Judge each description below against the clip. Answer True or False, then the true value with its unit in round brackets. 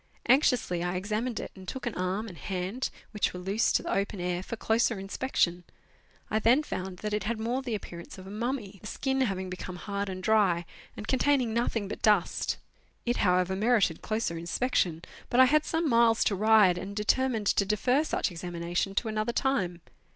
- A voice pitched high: True (210 Hz)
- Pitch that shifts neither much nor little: True (4.4 semitones)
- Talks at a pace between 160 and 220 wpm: True (195 wpm)